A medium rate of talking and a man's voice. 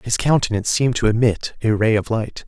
No: fast, 220 wpm; male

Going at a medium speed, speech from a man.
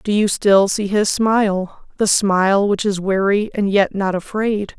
No: average, 190 wpm; female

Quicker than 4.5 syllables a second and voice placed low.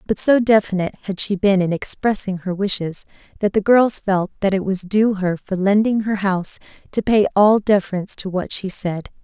No: 5.2 syllables/s; high, 195 Hz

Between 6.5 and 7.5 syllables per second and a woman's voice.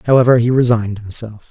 No: 6.6 syllables/s; male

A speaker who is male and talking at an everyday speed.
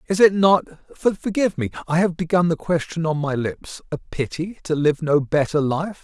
Yes: male; average, 180 wpm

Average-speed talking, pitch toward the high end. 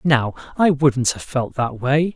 No: average, 195 wpm; medium, 140 Hz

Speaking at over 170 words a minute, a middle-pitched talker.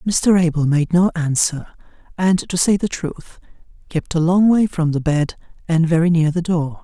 Yes: average, 195 wpm; medium, 170 Hz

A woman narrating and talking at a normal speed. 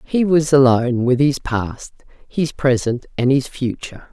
Yes: female; average, 160 wpm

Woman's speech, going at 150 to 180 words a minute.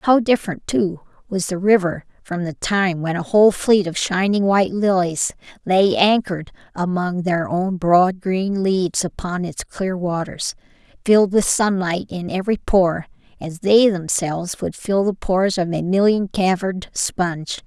Yes: female; average, 160 wpm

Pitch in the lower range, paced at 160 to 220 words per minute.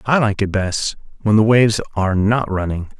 Yes: low, 105 Hz; average, 200 wpm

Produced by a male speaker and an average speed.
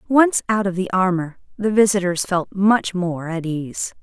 No: female; average, 180 wpm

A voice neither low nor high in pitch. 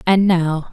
Yes: medium, 175 Hz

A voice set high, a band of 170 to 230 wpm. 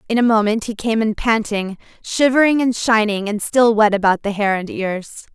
Yes: high, 220 Hz; average, 200 wpm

